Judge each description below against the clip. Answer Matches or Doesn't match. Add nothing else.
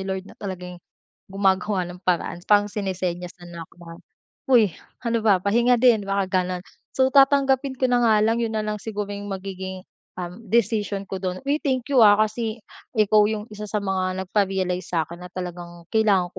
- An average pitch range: Matches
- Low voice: Doesn't match